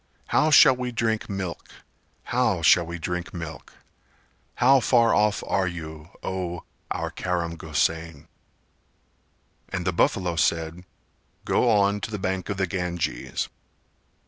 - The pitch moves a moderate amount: Yes, average, 3.7 semitones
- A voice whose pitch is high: No, very low, 90 Hz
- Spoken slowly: Yes, slow, 130 wpm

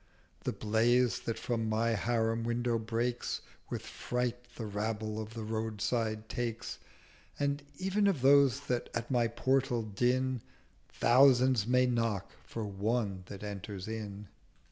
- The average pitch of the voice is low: Yes, low, 115 Hz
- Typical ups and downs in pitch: No, narrow, 2.3 semitones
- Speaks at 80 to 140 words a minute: Yes, slow, 135 wpm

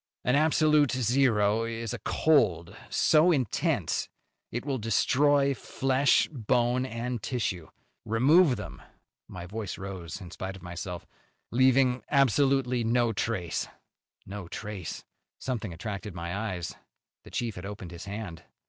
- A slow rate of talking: Yes, slow, 130 wpm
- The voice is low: Yes, low, 115 Hz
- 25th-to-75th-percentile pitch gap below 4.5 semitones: No, average, 5.2 semitones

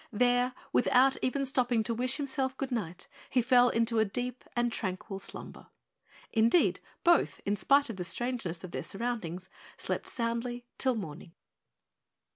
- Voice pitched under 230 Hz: No, high, 240 Hz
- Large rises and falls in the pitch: No, average, 3.9 semitones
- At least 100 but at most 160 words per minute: Yes, average, 145 wpm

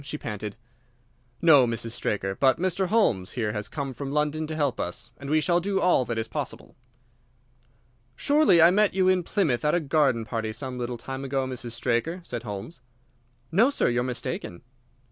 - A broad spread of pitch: Yes, wide, 6.2 semitones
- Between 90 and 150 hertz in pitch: Yes, low, 135 Hz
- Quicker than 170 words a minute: Yes, average, 185 wpm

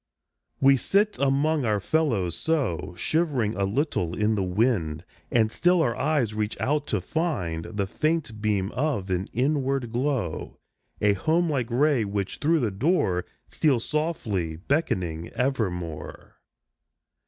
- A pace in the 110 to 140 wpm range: Yes, slow, 135 wpm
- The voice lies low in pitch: Yes, low, 115 Hz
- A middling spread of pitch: No, wide, 7.4 semitones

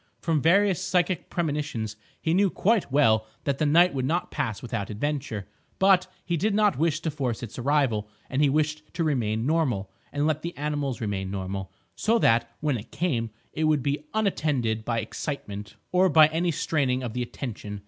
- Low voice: No, medium, 145 Hz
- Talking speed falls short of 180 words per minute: No, average, 185 wpm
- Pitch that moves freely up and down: Yes, wide, 6.3 semitones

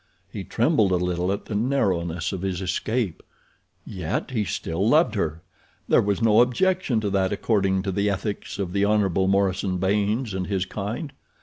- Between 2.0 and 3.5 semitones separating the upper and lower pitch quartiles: Yes, average, 2.7 semitones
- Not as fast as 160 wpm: No, average, 175 wpm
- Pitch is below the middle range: Yes, low, 100 Hz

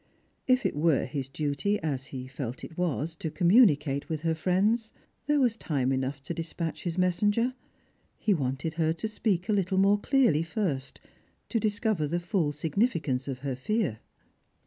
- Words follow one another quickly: No, average, 170 wpm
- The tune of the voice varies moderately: No, wide, 6.4 semitones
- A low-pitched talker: No, medium, 165 Hz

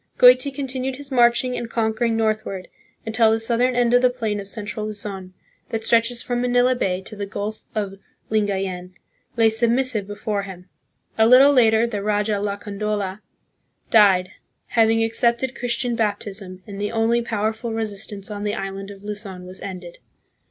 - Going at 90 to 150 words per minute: No, average, 160 wpm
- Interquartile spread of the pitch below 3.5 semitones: Yes, average, 2.8 semitones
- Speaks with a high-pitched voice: Yes, high, 220 Hz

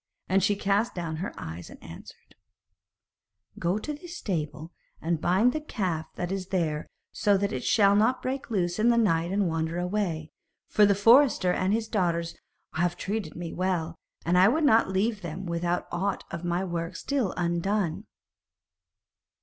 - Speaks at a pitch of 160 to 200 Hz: Yes, medium, 185 Hz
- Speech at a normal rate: Yes, average, 170 wpm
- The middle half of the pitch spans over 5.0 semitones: No, average, 3.7 semitones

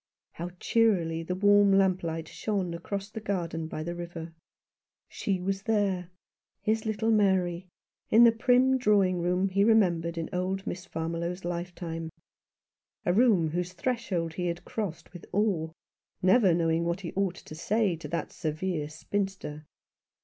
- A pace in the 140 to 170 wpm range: Yes, average, 150 wpm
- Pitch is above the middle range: No, medium, 180 Hz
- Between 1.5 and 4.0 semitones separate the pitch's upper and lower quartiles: Yes, average, 3.2 semitones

